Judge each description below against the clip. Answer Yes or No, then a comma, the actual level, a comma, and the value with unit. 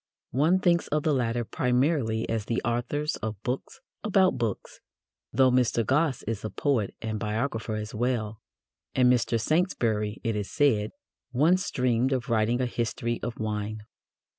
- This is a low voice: Yes, low, 120 Hz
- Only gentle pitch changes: No, average, 3.7 semitones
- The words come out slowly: No, average, 155 wpm